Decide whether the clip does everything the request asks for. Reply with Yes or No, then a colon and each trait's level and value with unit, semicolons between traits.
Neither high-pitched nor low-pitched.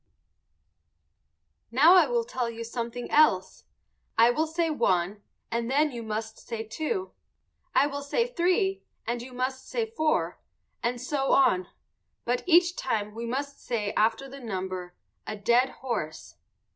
No: very high, 250 Hz